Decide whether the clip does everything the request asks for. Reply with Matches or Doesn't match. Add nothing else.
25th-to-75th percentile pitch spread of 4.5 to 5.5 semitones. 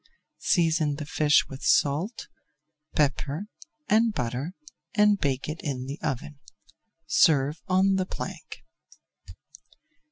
Matches